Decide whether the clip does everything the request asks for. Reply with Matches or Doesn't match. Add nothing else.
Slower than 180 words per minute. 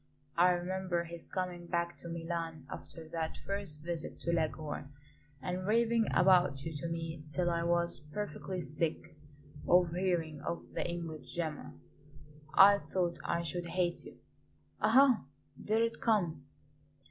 Matches